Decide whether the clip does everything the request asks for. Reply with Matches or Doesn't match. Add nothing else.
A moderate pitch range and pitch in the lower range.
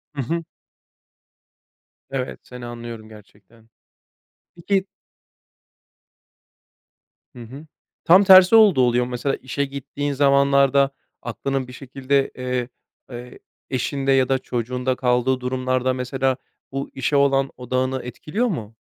Doesn't match